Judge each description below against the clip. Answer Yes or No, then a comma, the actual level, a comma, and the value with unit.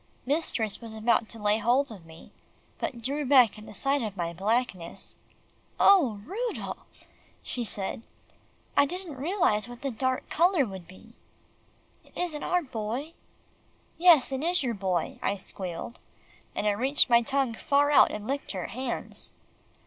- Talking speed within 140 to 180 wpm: Yes, average, 155 wpm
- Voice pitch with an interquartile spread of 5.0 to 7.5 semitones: Yes, average, 5.3 semitones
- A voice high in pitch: Yes, high, 245 Hz